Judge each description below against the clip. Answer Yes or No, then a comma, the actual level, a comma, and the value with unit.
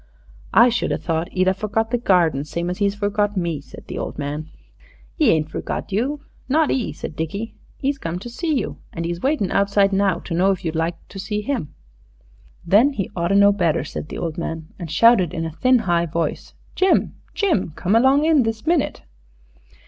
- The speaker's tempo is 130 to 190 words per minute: No, average, 200 wpm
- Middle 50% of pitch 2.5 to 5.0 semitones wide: No, wide, 5.6 semitones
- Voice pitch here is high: Yes, high, 195 Hz